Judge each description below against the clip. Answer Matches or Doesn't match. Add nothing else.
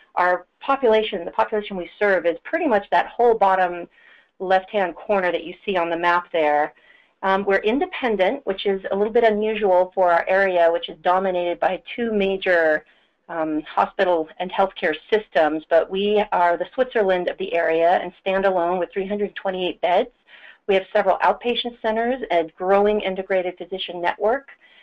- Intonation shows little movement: Doesn't match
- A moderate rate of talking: Matches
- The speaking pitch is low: Doesn't match